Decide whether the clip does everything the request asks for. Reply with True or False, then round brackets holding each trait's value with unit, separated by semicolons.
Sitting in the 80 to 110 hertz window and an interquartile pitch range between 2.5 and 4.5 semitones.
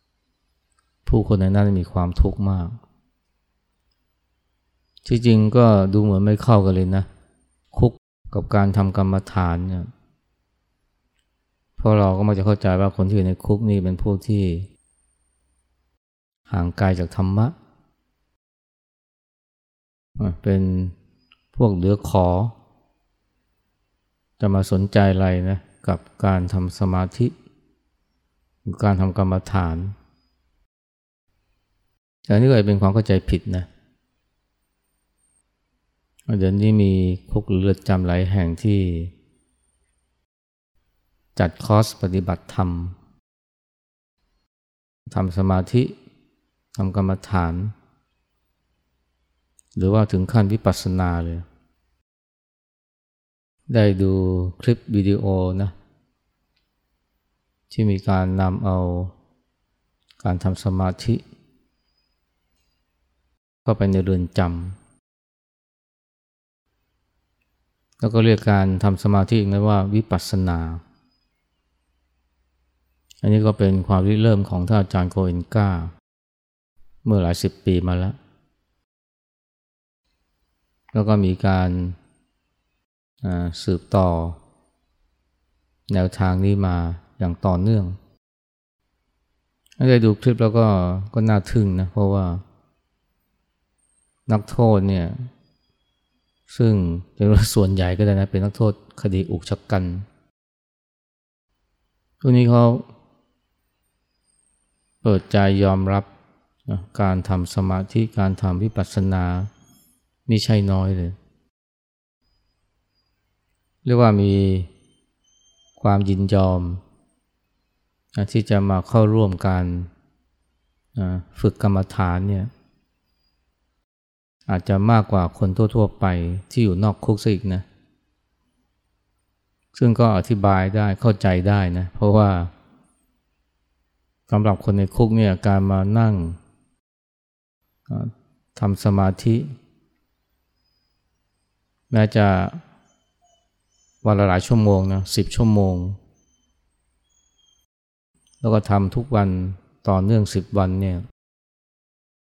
True (95 Hz; 3.6 semitones)